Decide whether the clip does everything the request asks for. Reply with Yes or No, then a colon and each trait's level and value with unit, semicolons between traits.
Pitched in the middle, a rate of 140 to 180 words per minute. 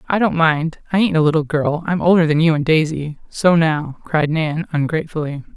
No: medium, 160 Hz; fast, 205 wpm